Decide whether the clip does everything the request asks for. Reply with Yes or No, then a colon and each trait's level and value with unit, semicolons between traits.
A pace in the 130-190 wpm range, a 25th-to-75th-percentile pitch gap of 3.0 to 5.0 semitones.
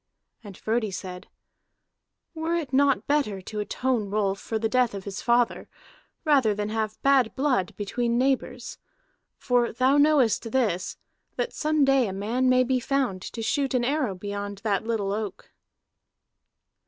Yes: average, 155 wpm; average, 4.5 semitones